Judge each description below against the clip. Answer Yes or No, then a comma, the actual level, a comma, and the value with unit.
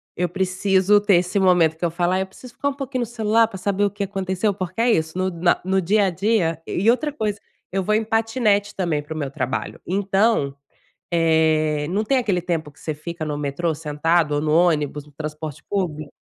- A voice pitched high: No, medium, 180 Hz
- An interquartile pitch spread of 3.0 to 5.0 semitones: Yes, average, 4.5 semitones